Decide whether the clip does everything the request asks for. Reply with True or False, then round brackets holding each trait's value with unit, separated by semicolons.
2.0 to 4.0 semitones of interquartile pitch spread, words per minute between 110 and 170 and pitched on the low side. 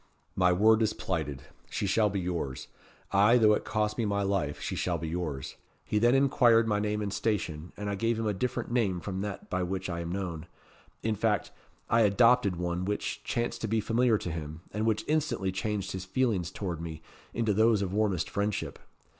False (3.7 semitones; 205 wpm; 100 Hz)